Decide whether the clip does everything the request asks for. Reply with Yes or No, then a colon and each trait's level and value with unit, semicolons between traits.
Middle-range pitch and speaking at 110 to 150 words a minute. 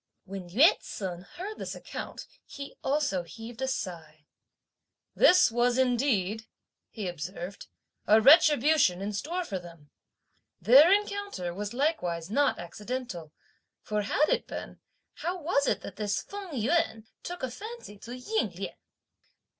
No: high, 235 Hz; average, 140 wpm